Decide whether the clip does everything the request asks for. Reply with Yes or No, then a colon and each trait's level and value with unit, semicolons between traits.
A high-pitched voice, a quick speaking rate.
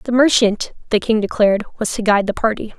Yes: high, 220 Hz; fast, 215 wpm